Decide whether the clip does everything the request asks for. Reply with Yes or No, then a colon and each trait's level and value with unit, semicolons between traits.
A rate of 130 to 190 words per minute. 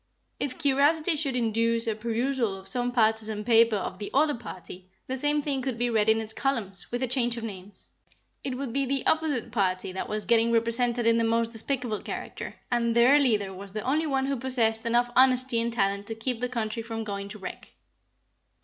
No: fast, 205 wpm